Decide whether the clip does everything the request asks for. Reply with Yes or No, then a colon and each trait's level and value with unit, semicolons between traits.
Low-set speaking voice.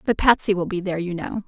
No: high, 190 Hz